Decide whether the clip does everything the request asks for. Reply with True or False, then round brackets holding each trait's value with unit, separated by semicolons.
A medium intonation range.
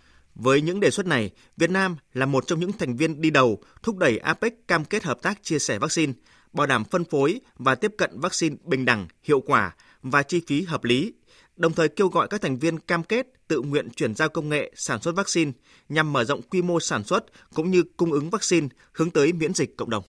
True (4.8 semitones)